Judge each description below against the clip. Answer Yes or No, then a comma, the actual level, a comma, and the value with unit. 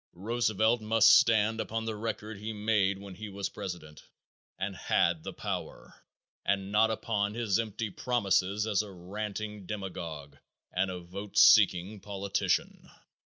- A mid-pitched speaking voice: No, low, 105 Hz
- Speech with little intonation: Yes, narrow, 2.3 semitones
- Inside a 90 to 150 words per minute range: Yes, average, 140 wpm